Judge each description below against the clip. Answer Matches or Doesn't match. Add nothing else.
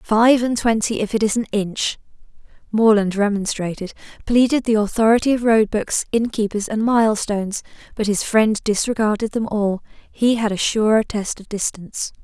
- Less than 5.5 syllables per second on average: Matches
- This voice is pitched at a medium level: Doesn't match